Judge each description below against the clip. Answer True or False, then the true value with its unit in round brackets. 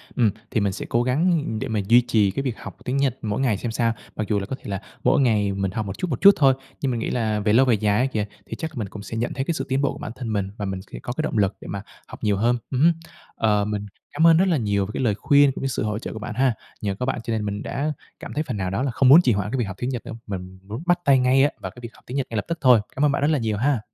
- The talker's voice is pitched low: True (120 Hz)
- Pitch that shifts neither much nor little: True (4.4 semitones)